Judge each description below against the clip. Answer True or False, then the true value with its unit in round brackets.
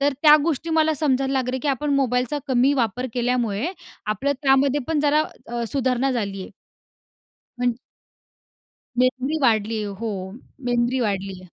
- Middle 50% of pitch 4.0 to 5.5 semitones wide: False (3.1 semitones)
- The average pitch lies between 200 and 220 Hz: False (255 Hz)